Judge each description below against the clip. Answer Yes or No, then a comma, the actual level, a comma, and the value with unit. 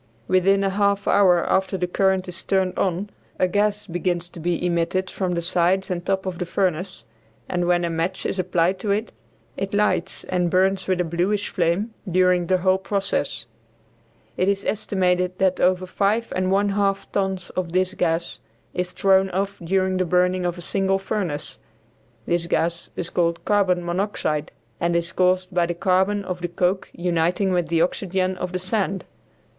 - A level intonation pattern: Yes, narrow, 1.7 semitones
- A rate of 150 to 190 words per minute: Yes, average, 180 wpm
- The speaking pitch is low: No, medium, 185 Hz